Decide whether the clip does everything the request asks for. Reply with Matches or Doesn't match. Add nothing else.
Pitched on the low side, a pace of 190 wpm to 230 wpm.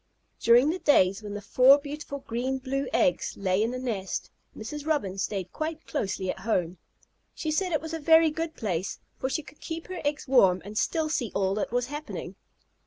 Doesn't match